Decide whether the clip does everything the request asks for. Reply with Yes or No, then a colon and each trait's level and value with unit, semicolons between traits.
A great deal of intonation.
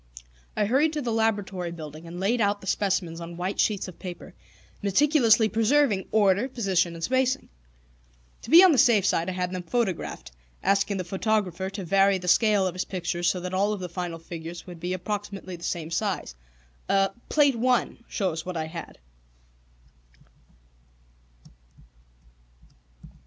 No: average, 3.8 semitones